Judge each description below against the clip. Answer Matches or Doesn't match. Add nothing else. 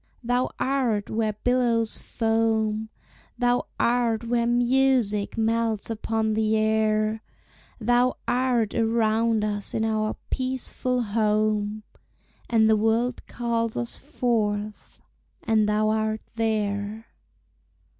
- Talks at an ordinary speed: Doesn't match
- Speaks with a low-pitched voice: Doesn't match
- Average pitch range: Doesn't match